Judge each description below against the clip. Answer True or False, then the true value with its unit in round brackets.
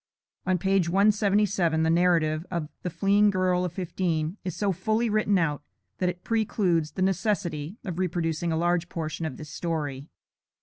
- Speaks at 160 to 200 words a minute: True (165 wpm)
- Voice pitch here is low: False (180 Hz)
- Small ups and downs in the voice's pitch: False (3.3 semitones)